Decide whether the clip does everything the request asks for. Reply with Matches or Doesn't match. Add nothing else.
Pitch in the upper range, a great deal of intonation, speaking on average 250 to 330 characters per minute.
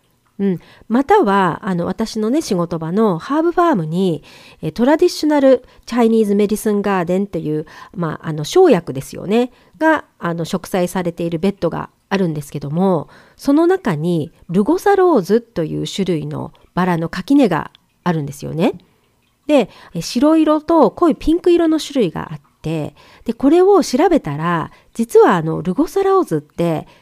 Matches